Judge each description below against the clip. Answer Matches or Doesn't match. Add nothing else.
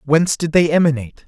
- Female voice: Doesn't match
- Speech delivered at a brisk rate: Doesn't match